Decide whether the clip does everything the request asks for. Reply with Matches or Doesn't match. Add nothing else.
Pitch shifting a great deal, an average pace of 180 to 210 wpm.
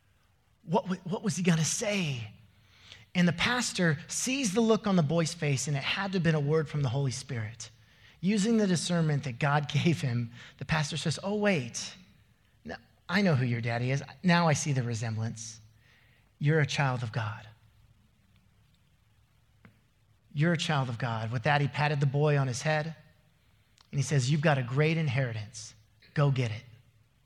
Matches